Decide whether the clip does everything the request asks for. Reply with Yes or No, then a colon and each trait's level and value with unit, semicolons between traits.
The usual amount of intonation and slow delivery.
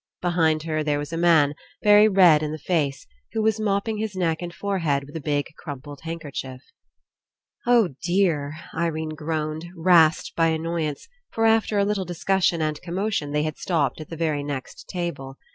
No: average, 3.6 semitones; average, 190 wpm